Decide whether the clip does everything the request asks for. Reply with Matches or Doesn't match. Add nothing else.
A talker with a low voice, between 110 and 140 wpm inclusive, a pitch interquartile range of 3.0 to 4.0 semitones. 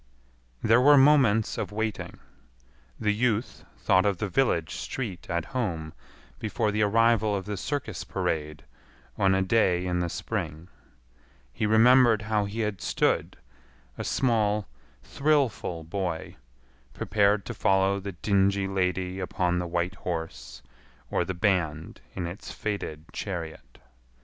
Matches